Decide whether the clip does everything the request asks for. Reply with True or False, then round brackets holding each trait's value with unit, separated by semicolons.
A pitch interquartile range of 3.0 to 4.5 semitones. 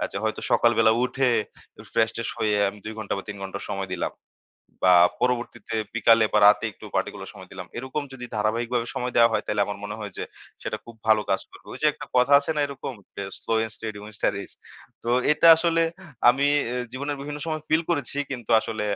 True (3.6 semitones)